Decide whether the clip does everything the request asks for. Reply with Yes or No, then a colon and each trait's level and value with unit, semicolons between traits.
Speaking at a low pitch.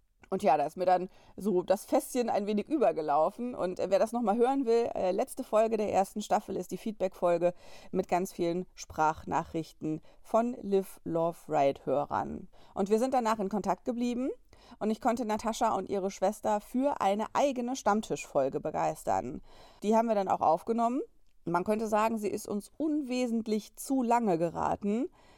No: high, 210 Hz